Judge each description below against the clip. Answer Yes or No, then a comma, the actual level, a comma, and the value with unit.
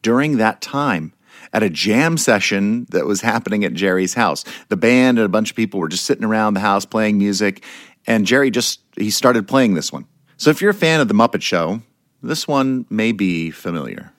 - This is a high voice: No, low, 110 Hz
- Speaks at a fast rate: Yes, fast, 210 wpm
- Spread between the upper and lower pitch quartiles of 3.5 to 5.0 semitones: Yes, average, 4.0 semitones